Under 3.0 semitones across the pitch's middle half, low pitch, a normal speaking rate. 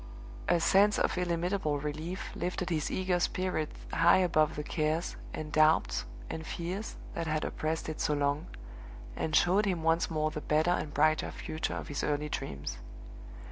No: narrow, 2.6 semitones; medium, 160 Hz; average, 165 wpm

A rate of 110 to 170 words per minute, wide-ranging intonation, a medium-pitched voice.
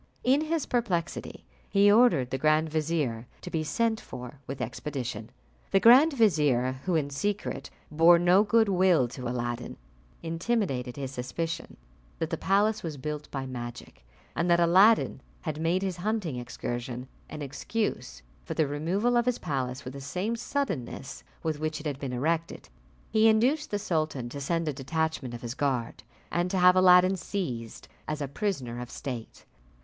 Yes: average, 165 wpm; wide, 6.8 semitones; medium, 160 Hz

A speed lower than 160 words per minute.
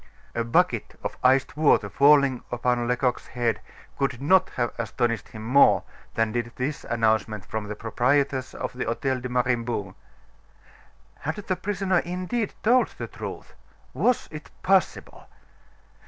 Yes: average, 140 wpm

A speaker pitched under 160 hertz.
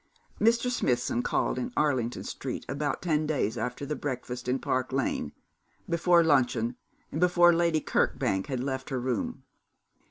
Yes: low, 135 Hz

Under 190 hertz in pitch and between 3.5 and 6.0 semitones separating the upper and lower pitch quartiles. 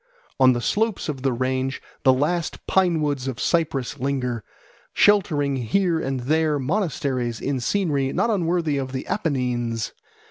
Yes: medium, 140 Hz; average, 4.3 semitones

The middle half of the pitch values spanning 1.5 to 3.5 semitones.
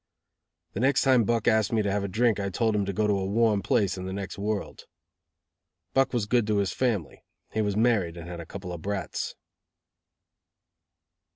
Yes: narrow, 2.6 semitones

